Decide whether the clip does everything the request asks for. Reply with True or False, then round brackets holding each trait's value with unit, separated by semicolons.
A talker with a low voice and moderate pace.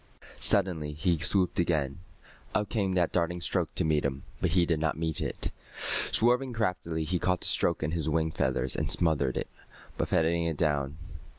True (85 Hz; 180 wpm)